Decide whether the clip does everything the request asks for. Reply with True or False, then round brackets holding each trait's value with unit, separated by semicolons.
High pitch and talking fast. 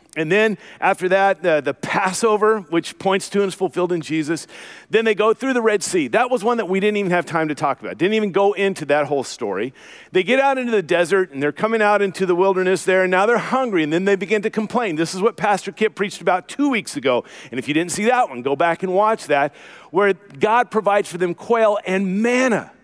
True (195 Hz; 250 wpm)